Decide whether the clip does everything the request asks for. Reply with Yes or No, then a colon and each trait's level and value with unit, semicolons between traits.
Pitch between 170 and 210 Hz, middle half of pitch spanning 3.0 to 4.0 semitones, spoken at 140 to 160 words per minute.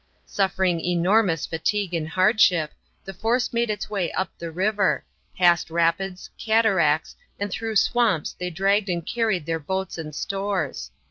Yes: high, 190 Hz; average, 3.7 semitones; average, 145 wpm